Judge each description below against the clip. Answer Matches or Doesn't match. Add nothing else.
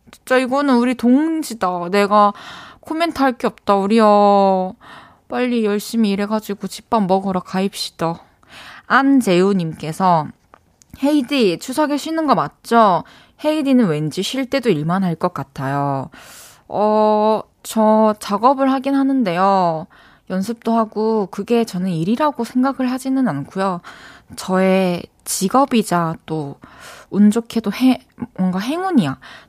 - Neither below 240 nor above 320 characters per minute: Matches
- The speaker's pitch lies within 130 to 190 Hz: Doesn't match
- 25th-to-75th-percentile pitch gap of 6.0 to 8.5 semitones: Doesn't match